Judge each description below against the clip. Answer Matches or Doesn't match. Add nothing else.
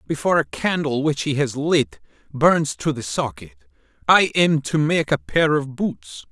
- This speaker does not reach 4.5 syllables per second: Matches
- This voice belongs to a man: Matches